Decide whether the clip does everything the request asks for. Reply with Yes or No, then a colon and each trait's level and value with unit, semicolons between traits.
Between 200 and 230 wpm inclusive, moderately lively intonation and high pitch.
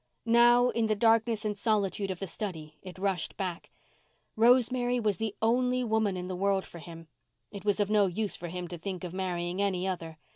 Yes: fast, 205 wpm; average, 3.6 semitones; high, 200 Hz